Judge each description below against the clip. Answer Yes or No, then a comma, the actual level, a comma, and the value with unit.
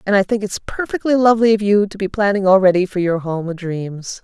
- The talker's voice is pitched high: Yes, high, 200 Hz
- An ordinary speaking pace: No, fast, 225 wpm